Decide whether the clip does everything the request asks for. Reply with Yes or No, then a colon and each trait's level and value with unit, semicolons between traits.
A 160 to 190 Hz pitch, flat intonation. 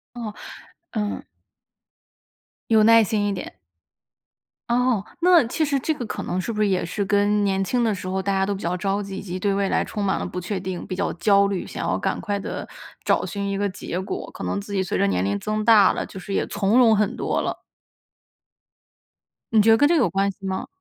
No: high, 200 Hz; narrow, 2.2 semitones